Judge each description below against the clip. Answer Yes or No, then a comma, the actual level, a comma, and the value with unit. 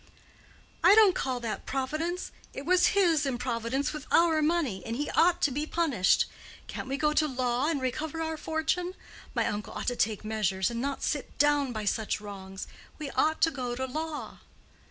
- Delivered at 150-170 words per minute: No, average, 185 wpm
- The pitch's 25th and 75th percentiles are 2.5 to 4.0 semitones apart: No, average, 4.9 semitones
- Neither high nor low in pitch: No, very high, 280 Hz